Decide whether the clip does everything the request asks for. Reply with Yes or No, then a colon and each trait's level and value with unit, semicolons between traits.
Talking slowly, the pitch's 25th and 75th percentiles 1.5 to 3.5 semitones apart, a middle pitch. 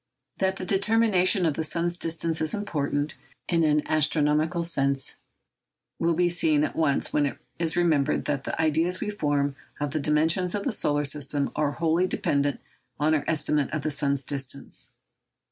No: average, 170 wpm; average, 2.9 semitones; medium, 155 Hz